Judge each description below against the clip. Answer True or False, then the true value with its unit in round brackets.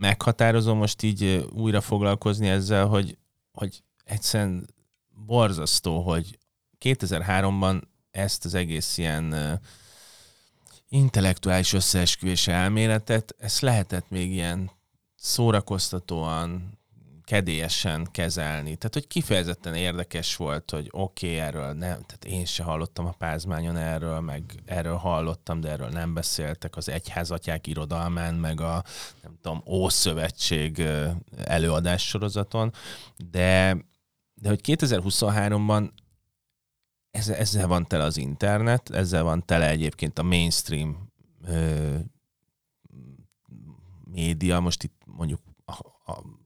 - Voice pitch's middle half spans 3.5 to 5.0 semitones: True (4.0 semitones)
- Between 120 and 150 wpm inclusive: False (105 wpm)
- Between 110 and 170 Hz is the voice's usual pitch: False (90 Hz)